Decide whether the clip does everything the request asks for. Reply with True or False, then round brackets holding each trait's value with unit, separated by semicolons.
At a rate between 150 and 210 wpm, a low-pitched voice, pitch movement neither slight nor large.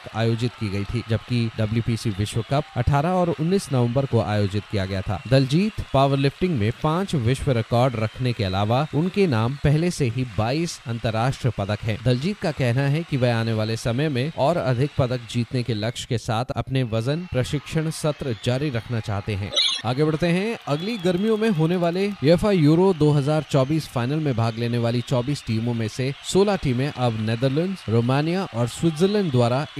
True (180 wpm; 130 Hz; 5.0 semitones)